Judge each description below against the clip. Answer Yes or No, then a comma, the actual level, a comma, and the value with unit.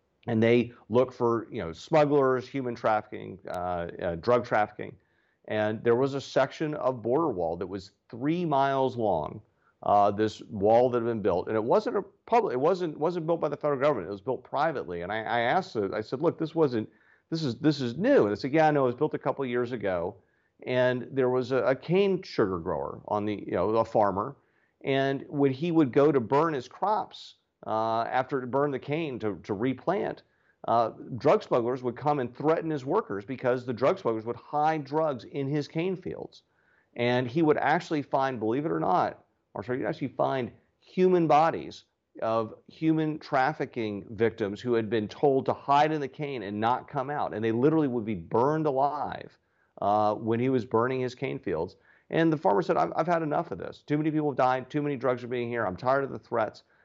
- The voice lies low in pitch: Yes, low, 130 Hz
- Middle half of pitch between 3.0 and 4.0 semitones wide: No, average, 4.7 semitones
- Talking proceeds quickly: Yes, fast, 215 wpm